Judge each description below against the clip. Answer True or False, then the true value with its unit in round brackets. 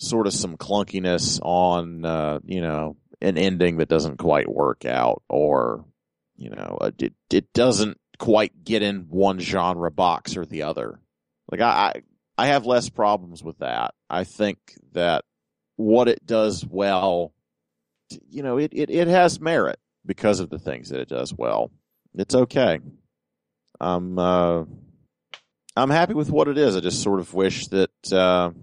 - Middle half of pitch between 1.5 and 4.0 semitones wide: True (3.5 semitones)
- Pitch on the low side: True (95 Hz)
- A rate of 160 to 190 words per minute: True (165 wpm)